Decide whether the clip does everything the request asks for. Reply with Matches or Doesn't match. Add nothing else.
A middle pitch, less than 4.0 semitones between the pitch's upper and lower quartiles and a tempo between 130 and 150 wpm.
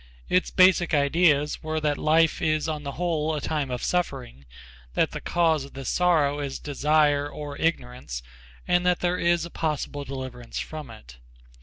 Doesn't match